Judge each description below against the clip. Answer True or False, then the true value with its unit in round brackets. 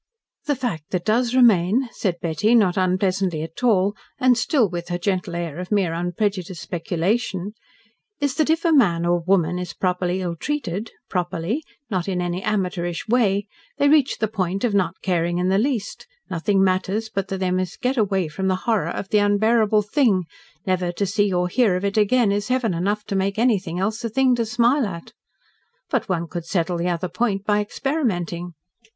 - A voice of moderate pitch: False (195 Hz)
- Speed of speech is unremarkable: True (190 wpm)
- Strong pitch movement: False (3.8 semitones)